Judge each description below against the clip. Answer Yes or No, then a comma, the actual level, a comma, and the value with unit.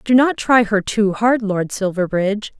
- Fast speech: No, average, 185 wpm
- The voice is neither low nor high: No, high, 210 Hz